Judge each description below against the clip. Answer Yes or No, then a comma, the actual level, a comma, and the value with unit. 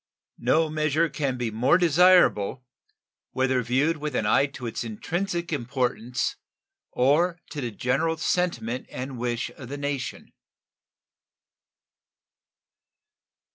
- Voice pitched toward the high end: No, low, 135 Hz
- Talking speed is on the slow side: Yes, slow, 110 wpm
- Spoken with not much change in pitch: No, average, 4.6 semitones